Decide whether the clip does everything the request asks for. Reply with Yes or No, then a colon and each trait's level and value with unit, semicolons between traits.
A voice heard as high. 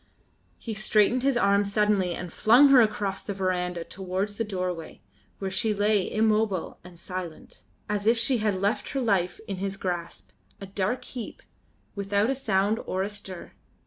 Yes: high, 200 Hz